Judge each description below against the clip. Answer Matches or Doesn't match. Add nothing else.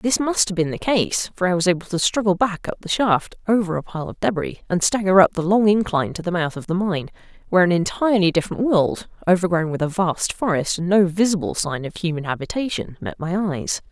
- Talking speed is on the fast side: Matches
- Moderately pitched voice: Matches